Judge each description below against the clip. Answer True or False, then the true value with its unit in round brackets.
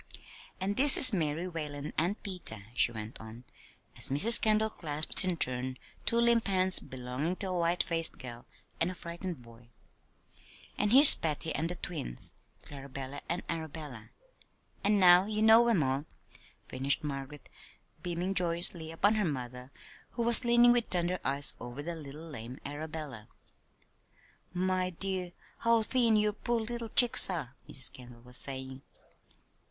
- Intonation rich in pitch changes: True (6.4 semitones)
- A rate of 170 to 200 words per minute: False (150 wpm)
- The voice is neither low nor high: True (165 Hz)